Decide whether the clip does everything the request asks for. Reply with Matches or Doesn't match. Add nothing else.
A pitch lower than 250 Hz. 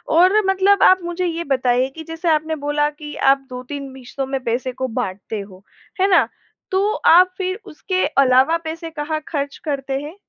Doesn't match